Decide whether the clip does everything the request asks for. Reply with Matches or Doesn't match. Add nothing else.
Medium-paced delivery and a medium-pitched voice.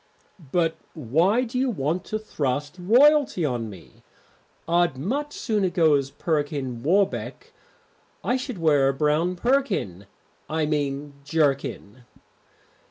Doesn't match